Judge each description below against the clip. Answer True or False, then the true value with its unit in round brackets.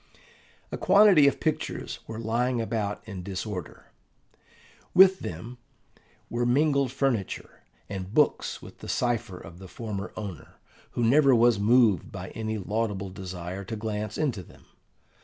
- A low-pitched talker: True (110 Hz)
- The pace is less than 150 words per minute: True (140 wpm)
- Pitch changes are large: False (4.2 semitones)